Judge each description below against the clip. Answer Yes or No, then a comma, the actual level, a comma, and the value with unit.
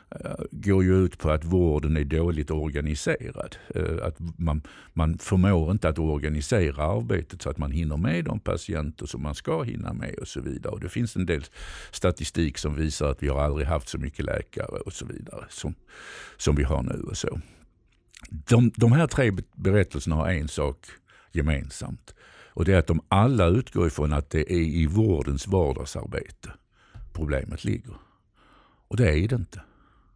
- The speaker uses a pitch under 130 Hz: Yes, very low, 85 Hz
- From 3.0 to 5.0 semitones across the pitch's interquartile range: Yes, average, 4.0 semitones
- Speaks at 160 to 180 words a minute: Yes, average, 175 wpm